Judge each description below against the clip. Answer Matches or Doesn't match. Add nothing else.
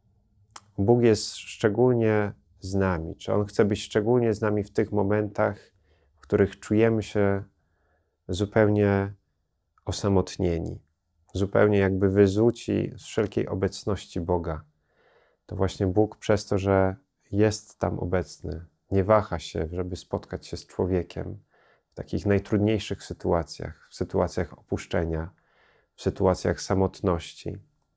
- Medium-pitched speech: Doesn't match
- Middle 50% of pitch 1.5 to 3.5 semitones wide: Matches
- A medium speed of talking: Matches